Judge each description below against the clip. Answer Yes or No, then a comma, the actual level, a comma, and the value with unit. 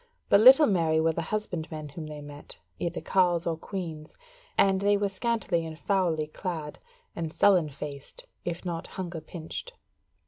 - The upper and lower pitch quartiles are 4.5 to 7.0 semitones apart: No, average, 3.4 semitones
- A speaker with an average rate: Yes, average, 160 wpm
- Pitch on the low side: No, medium, 170 Hz